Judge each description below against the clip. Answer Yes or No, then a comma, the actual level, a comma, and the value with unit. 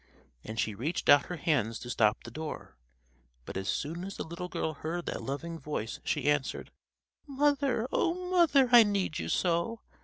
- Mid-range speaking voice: Yes, medium, 165 Hz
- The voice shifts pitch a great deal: Yes, wide, 8.6 semitones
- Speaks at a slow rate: No, average, 180 wpm